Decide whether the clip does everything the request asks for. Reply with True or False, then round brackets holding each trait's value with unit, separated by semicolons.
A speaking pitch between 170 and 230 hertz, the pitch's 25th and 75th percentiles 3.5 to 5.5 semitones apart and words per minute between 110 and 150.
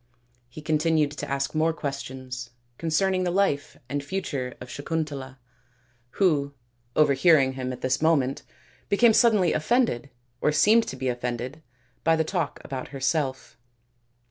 False (145 Hz; 3.8 semitones; 135 wpm)